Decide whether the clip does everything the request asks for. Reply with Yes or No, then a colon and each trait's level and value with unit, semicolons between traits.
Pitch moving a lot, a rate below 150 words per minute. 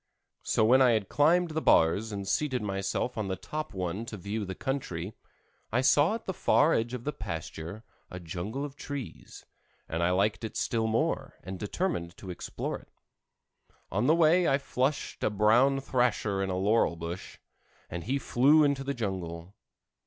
No: wide, 6.4 semitones; average, 180 wpm